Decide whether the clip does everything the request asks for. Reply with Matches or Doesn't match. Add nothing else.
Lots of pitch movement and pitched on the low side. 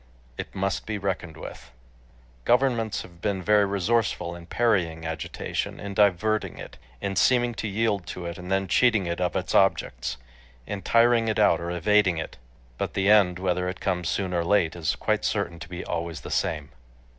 Doesn't match